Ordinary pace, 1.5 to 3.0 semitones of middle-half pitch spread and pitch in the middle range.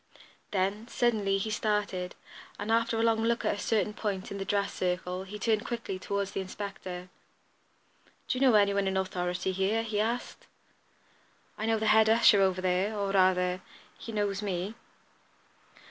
No: average, 170 wpm; narrow, 2.6 semitones; high, 200 Hz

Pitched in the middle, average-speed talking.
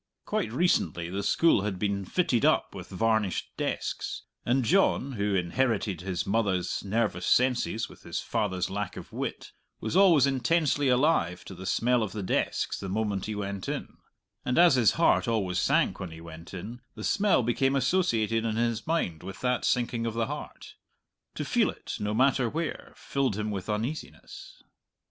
No: low, 110 Hz; average, 175 wpm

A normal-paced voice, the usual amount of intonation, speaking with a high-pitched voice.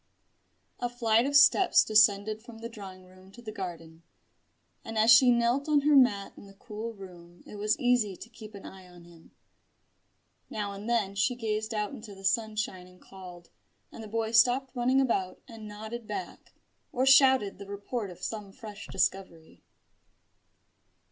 Yes: average, 170 wpm; average, 3.5 semitones; high, 215 Hz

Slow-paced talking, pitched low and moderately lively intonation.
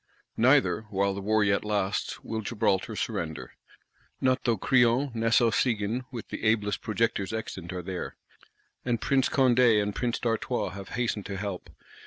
No: average, 155 wpm; low, 110 Hz; average, 3.3 semitones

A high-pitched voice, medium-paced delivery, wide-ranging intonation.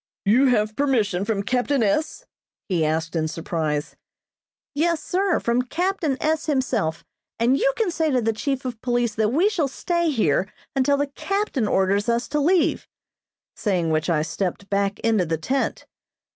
Yes: high, 240 Hz; average, 165 wpm; wide, 6.7 semitones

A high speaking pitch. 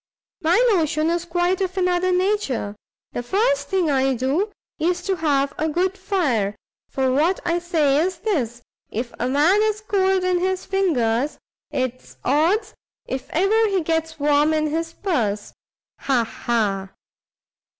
Yes: very high, 325 Hz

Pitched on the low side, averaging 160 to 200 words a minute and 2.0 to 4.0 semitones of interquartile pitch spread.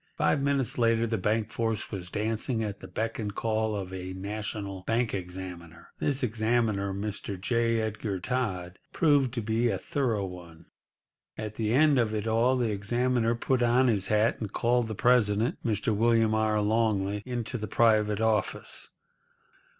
Yes: low, 110 Hz; average, 165 wpm; narrow, 2.6 semitones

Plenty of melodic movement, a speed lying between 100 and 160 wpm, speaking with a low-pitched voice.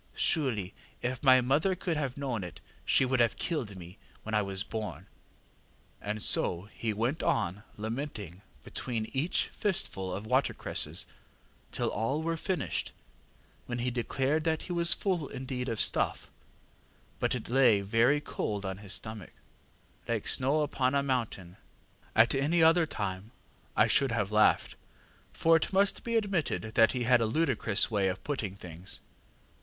Yes: wide, 6.0 semitones; average, 155 wpm; low, 125 Hz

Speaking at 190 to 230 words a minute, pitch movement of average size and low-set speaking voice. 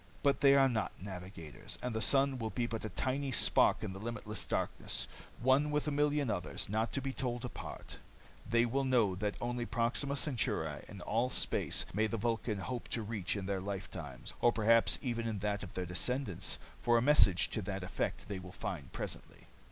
Yes: average, 200 wpm; average, 4.4 semitones; low, 115 Hz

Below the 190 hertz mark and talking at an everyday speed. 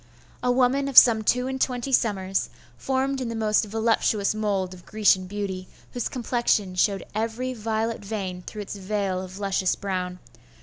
No: high, 215 Hz; average, 165 wpm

